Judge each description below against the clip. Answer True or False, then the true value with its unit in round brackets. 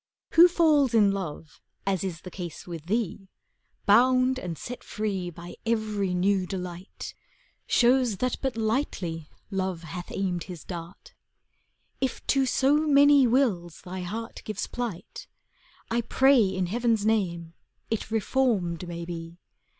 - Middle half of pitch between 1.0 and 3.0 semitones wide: False (5.6 semitones)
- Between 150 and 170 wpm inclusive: False (140 wpm)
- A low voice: False (200 Hz)